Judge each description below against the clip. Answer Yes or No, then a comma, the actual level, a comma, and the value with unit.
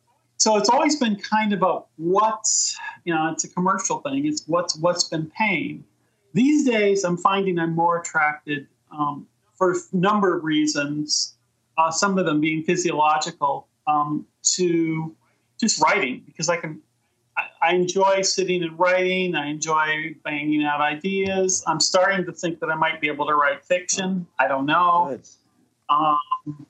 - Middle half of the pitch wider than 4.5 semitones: No, average, 4.0 semitones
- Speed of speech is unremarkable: Yes, average, 160 wpm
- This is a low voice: No, medium, 170 Hz